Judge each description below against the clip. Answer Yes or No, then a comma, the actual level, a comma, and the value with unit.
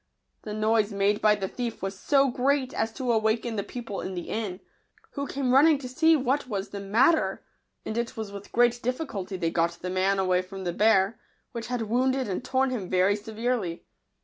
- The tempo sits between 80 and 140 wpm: No, fast, 205 wpm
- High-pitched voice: Yes, high, 220 Hz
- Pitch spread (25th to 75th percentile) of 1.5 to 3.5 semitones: No, average, 4.5 semitones